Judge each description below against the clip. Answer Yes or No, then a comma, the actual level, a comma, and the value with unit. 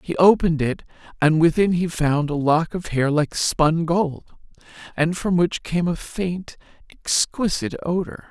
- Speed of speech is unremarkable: Yes, average, 160 wpm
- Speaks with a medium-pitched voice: Yes, medium, 165 Hz